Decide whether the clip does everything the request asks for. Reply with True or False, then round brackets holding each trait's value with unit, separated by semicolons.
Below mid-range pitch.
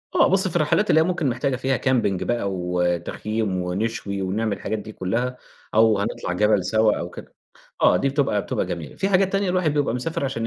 True (115 Hz)